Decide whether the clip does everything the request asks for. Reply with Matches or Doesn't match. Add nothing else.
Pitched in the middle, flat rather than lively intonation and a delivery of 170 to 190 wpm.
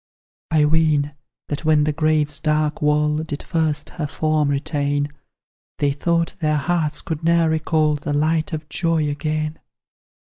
Doesn't match